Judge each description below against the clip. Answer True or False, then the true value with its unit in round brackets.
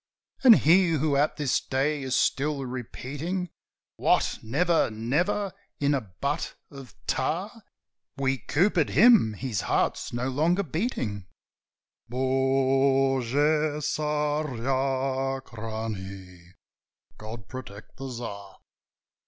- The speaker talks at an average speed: False (95 wpm)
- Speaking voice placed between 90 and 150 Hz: True (135 Hz)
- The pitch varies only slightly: False (4.2 semitones)